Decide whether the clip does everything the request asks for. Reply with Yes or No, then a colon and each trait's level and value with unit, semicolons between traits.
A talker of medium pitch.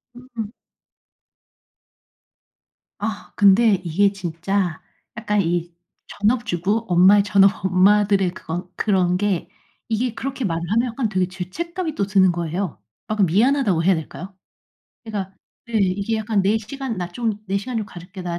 No: high, 200 Hz